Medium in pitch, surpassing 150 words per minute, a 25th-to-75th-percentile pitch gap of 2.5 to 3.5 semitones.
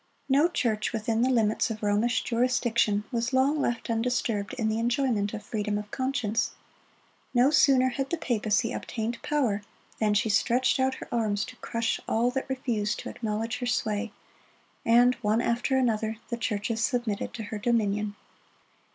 No: high, 230 Hz; average, 160 wpm; average, 2.8 semitones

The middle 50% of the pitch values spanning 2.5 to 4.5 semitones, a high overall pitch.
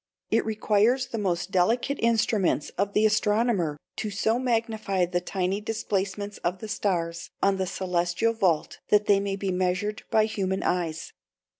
Yes: average, 3.1 semitones; high, 200 Hz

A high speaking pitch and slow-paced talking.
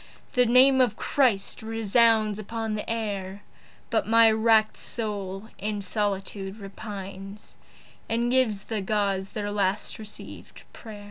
Yes: high, 215 Hz; slow, 125 wpm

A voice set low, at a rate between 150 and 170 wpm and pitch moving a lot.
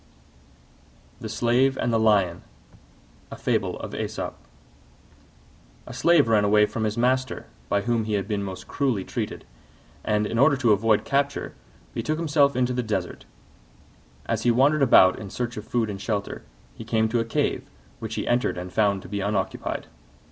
No: low, 110 Hz; average, 160 wpm; average, 3.5 semitones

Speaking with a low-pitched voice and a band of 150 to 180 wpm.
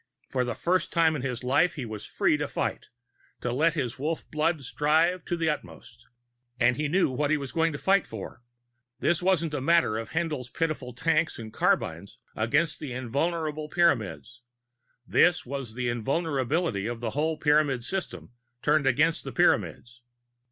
No: medium, 145 Hz; average, 165 wpm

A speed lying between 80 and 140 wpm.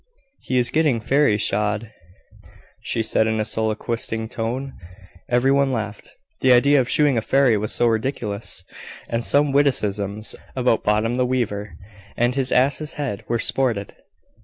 No: average, 150 wpm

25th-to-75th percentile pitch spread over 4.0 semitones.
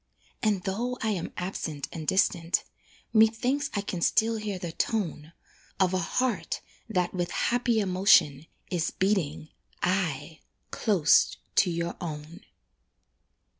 Yes: average, 4.4 semitones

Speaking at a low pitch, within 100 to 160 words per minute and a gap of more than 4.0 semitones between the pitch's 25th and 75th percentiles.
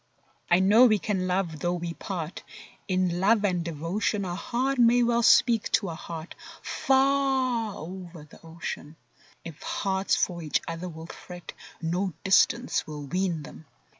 No: medium, 185 Hz; average, 155 wpm; average, 4.8 semitones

